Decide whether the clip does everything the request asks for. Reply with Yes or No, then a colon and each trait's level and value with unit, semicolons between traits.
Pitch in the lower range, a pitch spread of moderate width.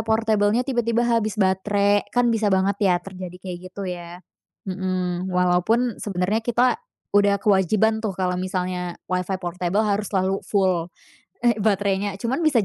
No: high, 195 Hz; average, 3.1 semitones